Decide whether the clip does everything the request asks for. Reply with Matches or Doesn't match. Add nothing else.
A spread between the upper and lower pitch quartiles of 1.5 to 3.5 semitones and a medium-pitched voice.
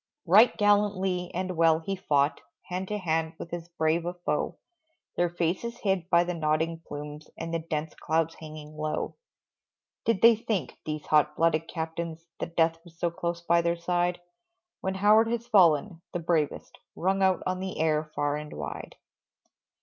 Matches